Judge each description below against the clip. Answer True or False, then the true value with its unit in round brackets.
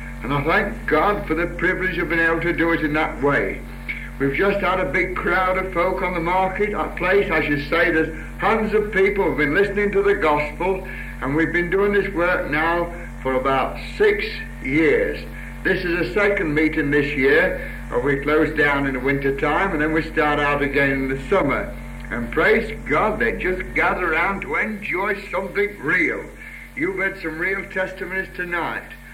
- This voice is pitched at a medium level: True (170 Hz)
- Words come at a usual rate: True (195 wpm)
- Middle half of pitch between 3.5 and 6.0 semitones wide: True (3.9 semitones)